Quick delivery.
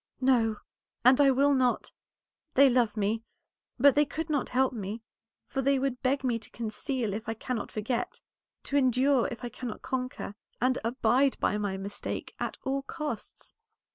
No: average, 170 wpm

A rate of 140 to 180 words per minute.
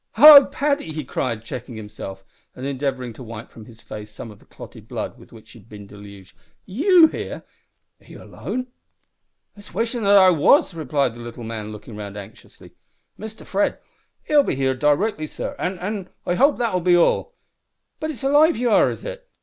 No: average, 190 wpm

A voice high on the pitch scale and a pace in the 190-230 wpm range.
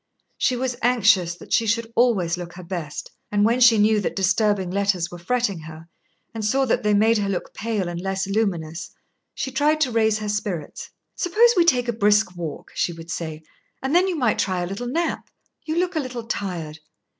Yes: high, 210 Hz; fast, 205 wpm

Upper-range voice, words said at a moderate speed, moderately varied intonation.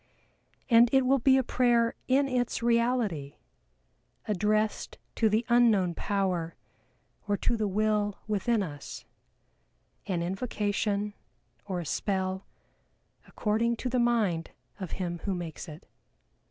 No: high, 210 Hz; slow, 125 wpm; average, 4.0 semitones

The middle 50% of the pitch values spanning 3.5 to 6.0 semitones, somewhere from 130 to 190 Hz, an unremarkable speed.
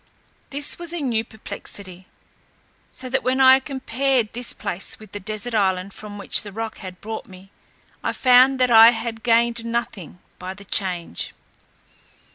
No: average, 4.1 semitones; high, 225 Hz; average, 160 wpm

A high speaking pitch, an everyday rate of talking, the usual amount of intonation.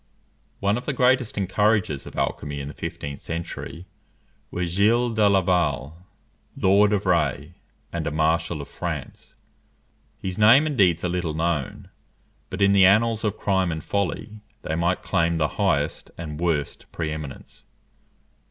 No: very low, 90 Hz; average, 150 wpm; average, 4.5 semitones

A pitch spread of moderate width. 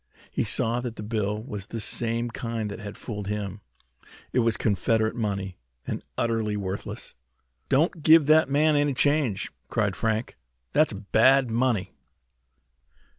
Yes: average, 3.8 semitones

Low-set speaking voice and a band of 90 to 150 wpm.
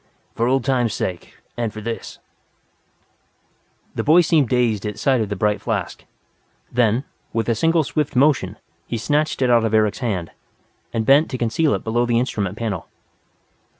No: low, 120 Hz; average, 175 wpm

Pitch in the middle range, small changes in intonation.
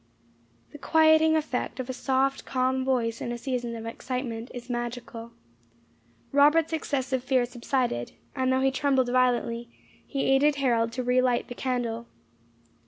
No: very high, 255 Hz; narrow, 2.0 semitones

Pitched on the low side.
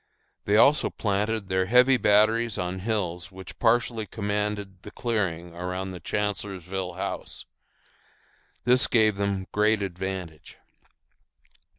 Yes: low, 100 Hz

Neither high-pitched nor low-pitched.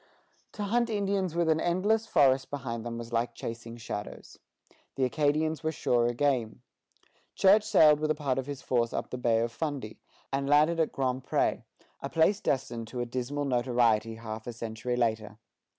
No: low, 130 Hz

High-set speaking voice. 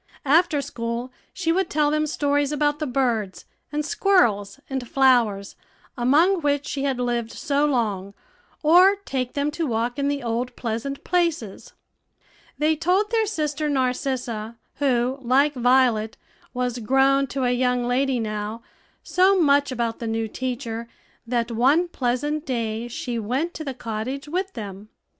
Yes: very high, 260 Hz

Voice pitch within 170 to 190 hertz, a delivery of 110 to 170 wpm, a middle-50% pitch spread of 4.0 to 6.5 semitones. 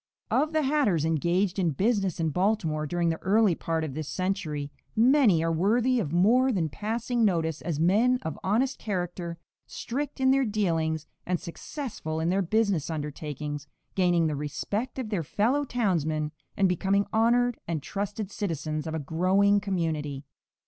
Yes: medium, 185 Hz; average, 165 wpm; wide, 5.4 semitones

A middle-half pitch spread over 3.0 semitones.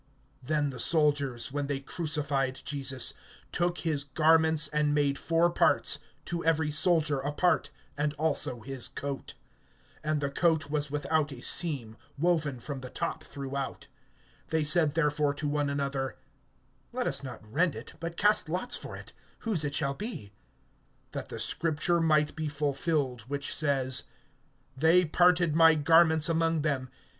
No: average, 2.7 semitones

